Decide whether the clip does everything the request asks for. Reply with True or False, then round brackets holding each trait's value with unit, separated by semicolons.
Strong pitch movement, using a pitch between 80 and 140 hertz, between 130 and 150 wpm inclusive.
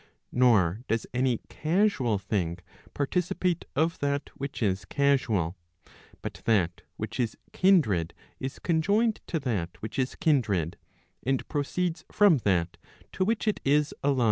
True (7.5 semitones; 135 Hz; 135 wpm)